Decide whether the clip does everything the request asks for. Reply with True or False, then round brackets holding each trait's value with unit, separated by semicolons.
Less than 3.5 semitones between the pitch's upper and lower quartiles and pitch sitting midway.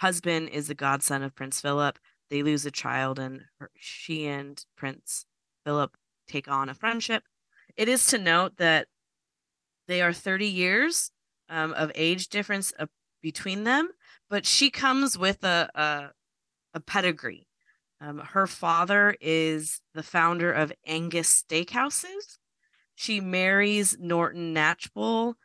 False (5.4 semitones; 170 Hz)